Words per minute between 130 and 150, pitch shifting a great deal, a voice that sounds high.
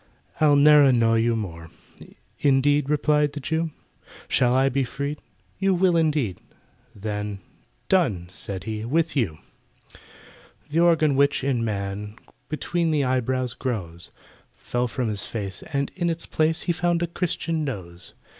No: average, 145 wpm; wide, 6.2 semitones; low, 135 Hz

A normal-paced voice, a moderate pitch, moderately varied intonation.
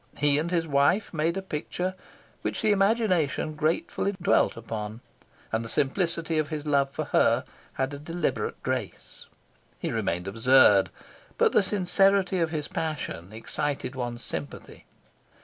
No: average, 145 wpm; medium, 150 Hz; wide, 5.7 semitones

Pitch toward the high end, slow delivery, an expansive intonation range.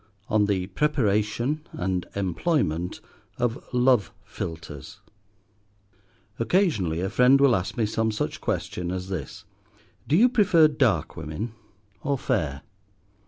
No: low, 105 Hz; slow, 115 wpm; wide, 6.7 semitones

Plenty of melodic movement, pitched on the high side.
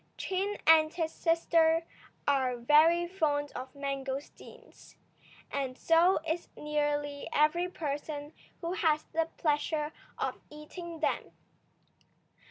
No: narrow, 2.5 semitones; very high, 305 Hz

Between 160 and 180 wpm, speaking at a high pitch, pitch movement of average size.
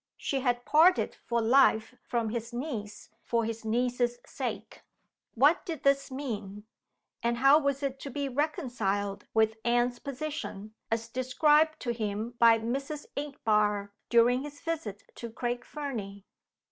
No: average, 140 wpm; high, 240 Hz; average, 4.0 semitones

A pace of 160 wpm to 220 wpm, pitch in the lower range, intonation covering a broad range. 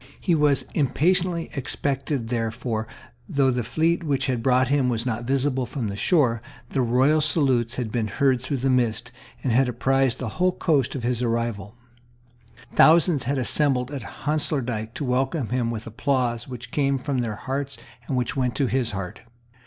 No: average, 175 wpm; low, 130 Hz; average, 3.1 semitones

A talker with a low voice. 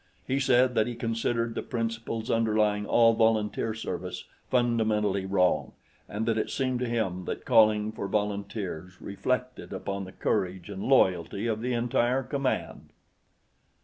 Yes: low, 110 Hz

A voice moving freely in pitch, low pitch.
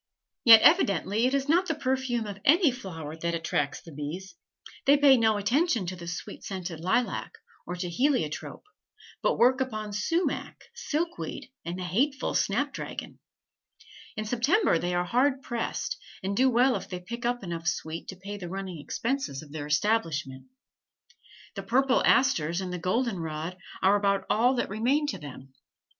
No: wide, 6.9 semitones; high, 205 Hz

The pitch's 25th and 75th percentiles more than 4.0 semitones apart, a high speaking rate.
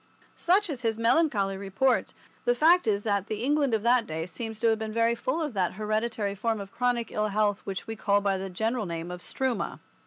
No: average, 3.4 semitones; fast, 220 wpm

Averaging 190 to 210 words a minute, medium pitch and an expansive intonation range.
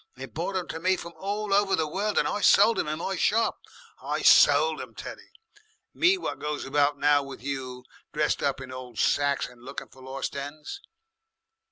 Yes: average, 195 wpm; medium, 150 Hz; wide, 6.1 semitones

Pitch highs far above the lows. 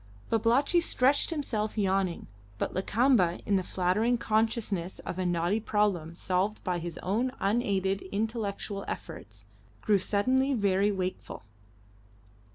No: average, 3.5 semitones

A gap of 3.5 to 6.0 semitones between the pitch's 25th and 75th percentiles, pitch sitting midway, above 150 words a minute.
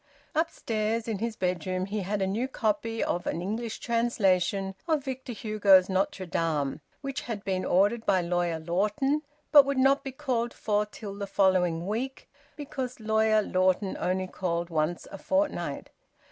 No: average, 4.3 semitones; high, 210 Hz; average, 160 wpm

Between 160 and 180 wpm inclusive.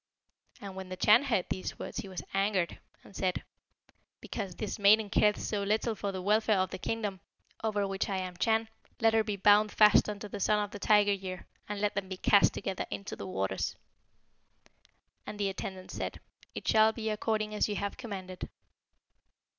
No: average, 190 wpm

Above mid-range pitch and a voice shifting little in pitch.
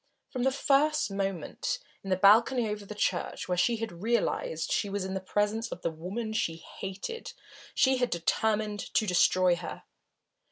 No: high, 205 Hz; average, 3.8 semitones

